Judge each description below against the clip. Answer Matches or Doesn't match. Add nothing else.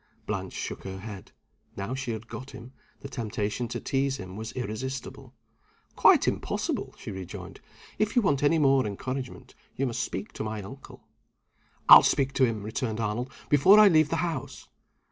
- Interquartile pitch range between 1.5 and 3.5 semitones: Doesn't match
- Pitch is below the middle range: Matches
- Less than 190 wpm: Matches